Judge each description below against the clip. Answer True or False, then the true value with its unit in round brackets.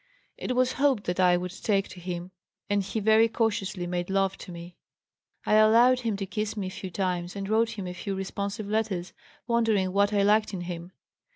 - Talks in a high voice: True (200 Hz)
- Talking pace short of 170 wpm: False (205 wpm)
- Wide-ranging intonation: False (3.1 semitones)